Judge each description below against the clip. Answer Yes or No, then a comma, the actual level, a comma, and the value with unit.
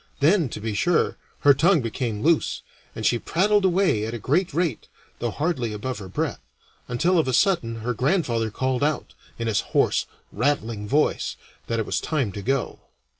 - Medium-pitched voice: No, low, 130 Hz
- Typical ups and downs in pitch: No, wide, 6.2 semitones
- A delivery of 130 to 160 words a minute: No, average, 180 wpm